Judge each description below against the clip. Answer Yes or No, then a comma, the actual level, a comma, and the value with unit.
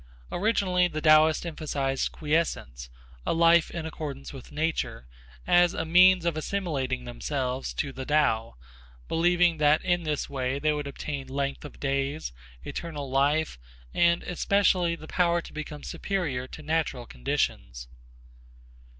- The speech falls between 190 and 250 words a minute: No, slow, 135 wpm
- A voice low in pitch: No, medium, 155 Hz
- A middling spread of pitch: Yes, average, 3.8 semitones